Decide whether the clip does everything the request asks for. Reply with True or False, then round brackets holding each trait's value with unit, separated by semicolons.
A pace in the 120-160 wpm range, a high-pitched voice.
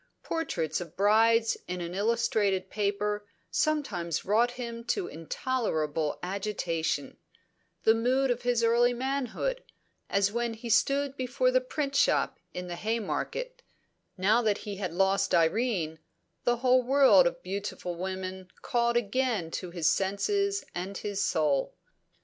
True (135 wpm; 220 Hz)